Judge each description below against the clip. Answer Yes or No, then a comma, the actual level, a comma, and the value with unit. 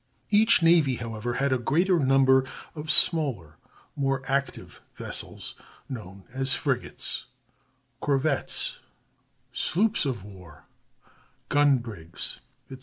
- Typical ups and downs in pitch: Yes, average, 4.5 semitones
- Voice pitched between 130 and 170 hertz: Yes, low, 135 Hz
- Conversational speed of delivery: No, slow, 105 wpm